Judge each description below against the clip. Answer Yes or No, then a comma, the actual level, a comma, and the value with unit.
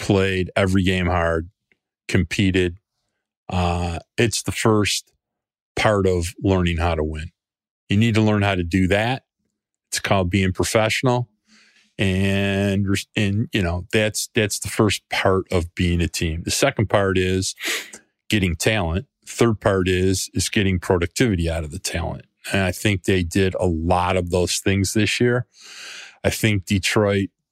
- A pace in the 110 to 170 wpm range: Yes, average, 155 wpm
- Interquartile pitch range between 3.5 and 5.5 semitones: No, narrow, 2.6 semitones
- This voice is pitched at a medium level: No, very low, 95 Hz